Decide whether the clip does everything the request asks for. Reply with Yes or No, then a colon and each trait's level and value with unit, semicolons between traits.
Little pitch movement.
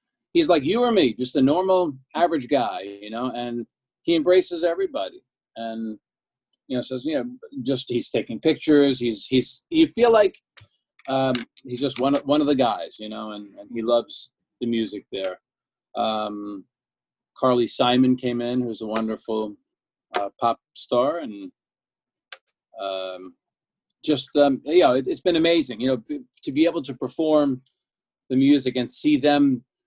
No: average, 4.6 semitones